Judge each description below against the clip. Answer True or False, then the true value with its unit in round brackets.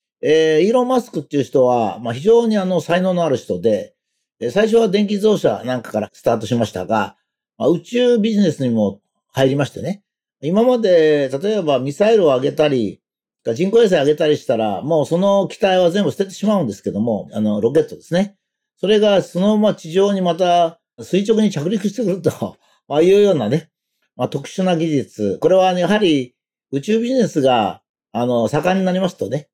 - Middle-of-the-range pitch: True (180 Hz)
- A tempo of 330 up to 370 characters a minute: False (380 characters per minute)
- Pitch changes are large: True (6.7 semitones)